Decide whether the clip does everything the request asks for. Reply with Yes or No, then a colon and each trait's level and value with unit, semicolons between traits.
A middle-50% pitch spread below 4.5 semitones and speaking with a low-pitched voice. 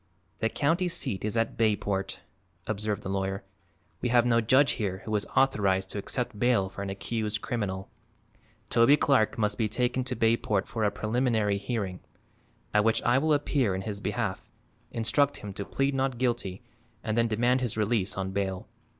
Yes: average, 3.6 semitones; low, 110 Hz